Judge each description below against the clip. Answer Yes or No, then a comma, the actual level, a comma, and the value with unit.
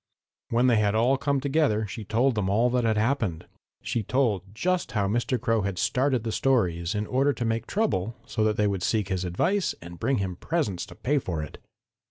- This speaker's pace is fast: Yes, fast, 215 wpm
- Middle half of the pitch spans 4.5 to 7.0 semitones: Yes, average, 4.8 semitones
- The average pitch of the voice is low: Yes, low, 110 Hz